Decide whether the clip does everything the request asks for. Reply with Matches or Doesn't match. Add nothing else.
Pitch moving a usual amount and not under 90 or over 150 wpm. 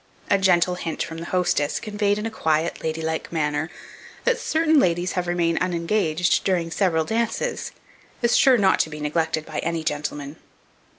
Doesn't match